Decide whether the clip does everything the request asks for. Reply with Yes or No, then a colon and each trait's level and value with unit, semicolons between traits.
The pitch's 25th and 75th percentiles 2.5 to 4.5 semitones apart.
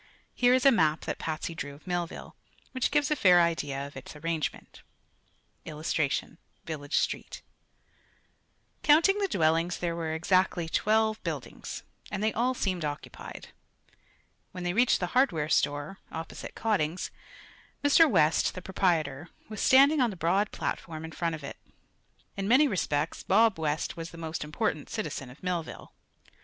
No: wide, 5.6 semitones